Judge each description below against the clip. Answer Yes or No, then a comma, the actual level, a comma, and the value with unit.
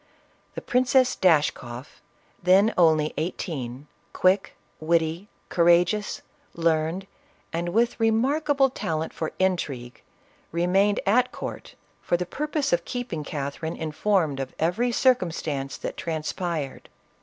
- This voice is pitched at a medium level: Yes, medium, 175 Hz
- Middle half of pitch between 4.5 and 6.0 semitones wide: Yes, average, 5.2 semitones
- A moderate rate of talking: No, slow, 110 wpm